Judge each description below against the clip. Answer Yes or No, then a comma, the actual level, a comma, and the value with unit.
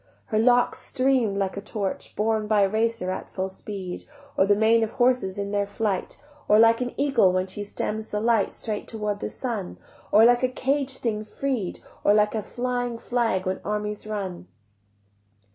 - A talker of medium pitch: No, high, 215 Hz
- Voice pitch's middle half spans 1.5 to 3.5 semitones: Yes, average, 3.0 semitones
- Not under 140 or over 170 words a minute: No, average, 190 wpm